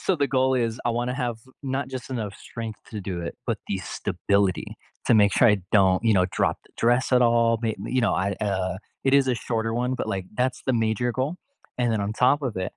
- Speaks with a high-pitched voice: No, low, 115 Hz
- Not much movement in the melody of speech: No, average, 3.7 semitones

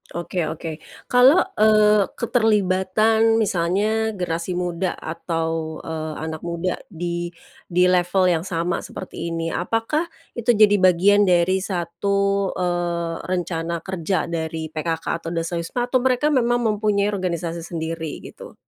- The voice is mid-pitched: Yes, medium, 180 Hz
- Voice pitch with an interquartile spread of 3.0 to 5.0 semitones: Yes, average, 3.7 semitones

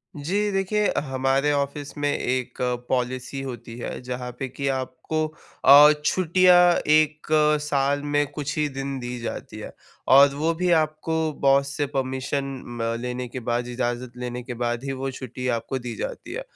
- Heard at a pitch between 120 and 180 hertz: Yes, low, 135 Hz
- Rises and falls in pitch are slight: No, average, 3.0 semitones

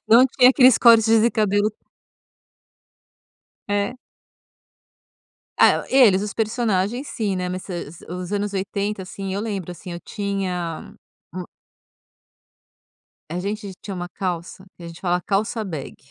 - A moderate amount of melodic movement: Yes, average, 3.1 semitones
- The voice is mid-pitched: No, high, 200 Hz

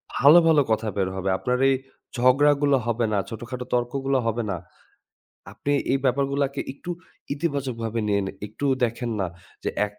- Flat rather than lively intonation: No, average, 3.5 semitones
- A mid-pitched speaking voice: No, low, 125 Hz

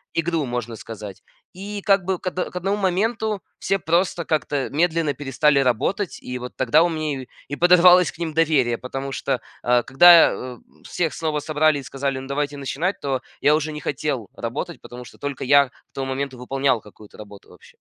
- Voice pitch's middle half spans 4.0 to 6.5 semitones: Yes, average, 4.6 semitones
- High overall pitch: No, medium, 145 Hz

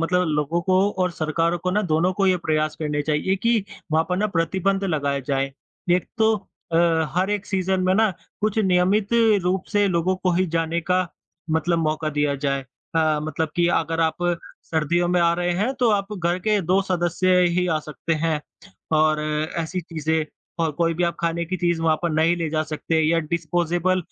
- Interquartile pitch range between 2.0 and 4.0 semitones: Yes, narrow, 2.6 semitones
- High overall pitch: No, medium, 170 Hz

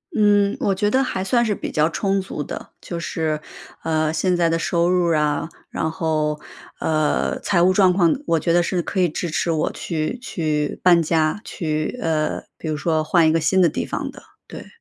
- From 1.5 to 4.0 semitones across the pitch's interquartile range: Yes, average, 3.0 semitones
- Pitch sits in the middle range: Yes, medium, 165 Hz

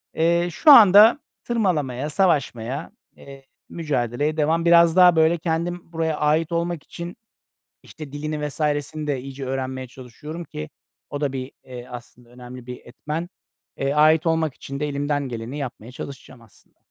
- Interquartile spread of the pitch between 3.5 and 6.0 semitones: Yes, average, 4.1 semitones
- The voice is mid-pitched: Yes, medium, 150 Hz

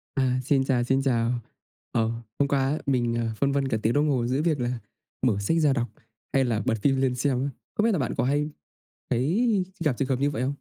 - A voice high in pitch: No, low, 135 Hz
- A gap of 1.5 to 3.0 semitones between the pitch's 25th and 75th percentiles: Yes, average, 2.7 semitones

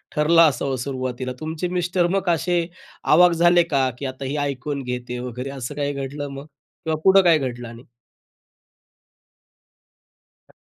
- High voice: No, medium, 145 Hz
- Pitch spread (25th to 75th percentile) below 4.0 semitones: No, average, 4.6 semitones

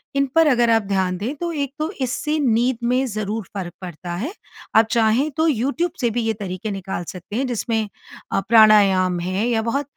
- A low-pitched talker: No, high, 225 Hz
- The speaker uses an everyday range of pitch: Yes, average, 4.9 semitones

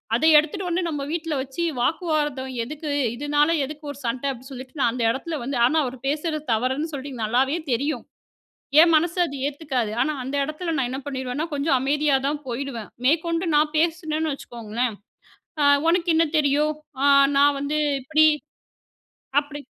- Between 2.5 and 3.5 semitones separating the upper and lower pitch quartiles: Yes, average, 3.0 semitones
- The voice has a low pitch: No, very high, 290 Hz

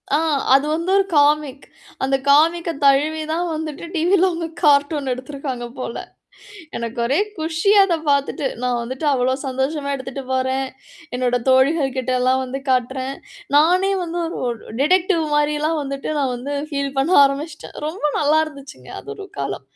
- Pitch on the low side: No, very high, 280 Hz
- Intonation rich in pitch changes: No, average, 3.3 semitones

